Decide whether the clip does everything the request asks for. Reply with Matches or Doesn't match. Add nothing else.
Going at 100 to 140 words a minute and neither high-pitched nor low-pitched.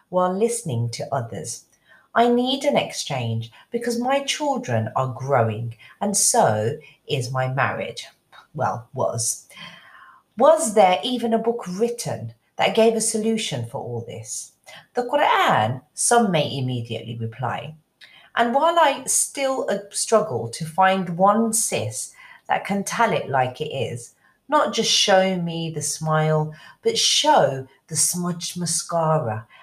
Matches